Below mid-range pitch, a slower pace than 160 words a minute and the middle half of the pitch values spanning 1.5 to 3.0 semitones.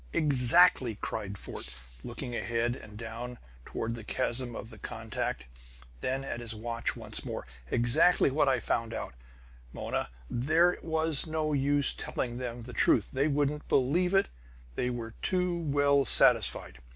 No: low, 130 Hz; average, 150 wpm; average, 4.3 semitones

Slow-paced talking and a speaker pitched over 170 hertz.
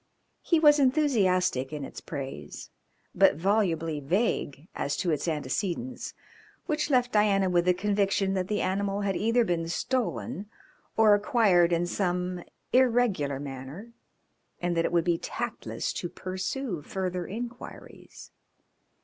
Yes: slow, 130 wpm; medium, 185 Hz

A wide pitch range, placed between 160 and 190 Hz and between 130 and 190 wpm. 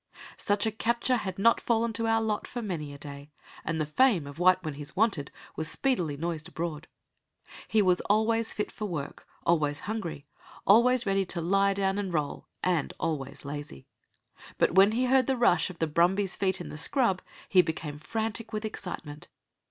Yes: wide, 5.8 semitones; medium, 185 Hz; average, 185 wpm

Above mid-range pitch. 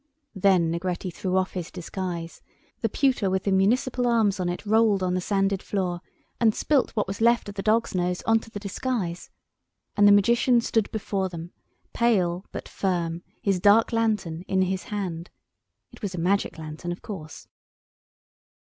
Yes: high, 195 Hz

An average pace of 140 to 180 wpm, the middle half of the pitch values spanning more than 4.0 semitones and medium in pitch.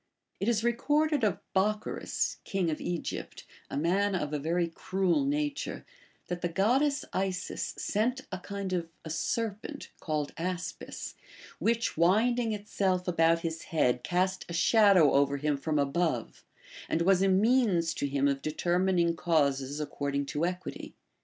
Yes: average, 145 wpm; average, 4.6 semitones; medium, 180 Hz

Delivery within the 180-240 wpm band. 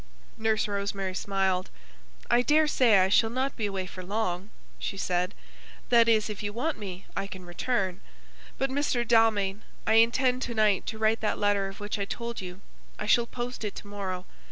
Yes: average, 185 wpm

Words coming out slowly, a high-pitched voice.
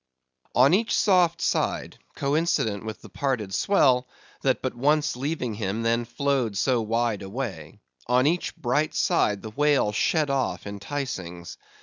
No: slow, 130 wpm; low, 125 Hz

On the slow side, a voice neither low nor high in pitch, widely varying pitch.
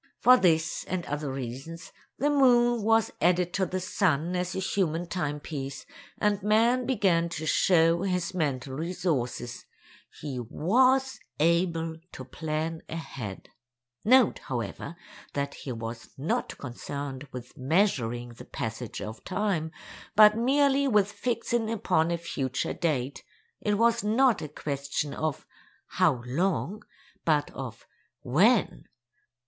Yes: slow, 125 wpm; medium, 165 Hz; wide, 6.9 semitones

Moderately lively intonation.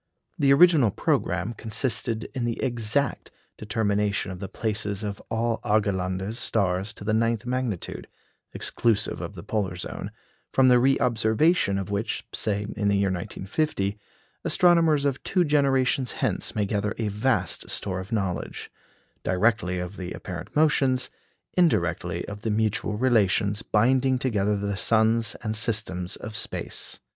Yes: average, 3.8 semitones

